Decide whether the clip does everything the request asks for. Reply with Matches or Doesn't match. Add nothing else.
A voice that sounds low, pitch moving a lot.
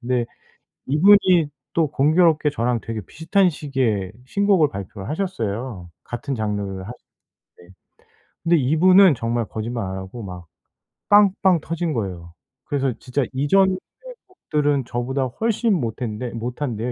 Matches